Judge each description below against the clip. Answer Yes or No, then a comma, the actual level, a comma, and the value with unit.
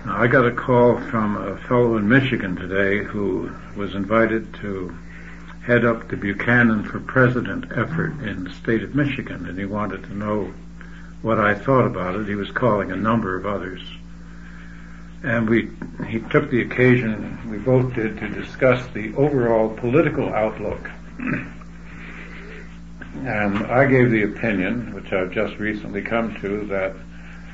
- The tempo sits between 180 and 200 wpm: No, average, 155 wpm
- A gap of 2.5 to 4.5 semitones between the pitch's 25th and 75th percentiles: Yes, average, 4.1 semitones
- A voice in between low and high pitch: No, low, 110 Hz